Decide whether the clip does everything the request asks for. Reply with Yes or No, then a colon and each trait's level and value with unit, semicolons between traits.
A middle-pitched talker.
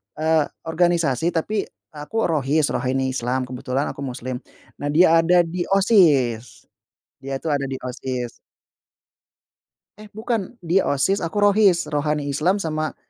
Yes: medium, 155 Hz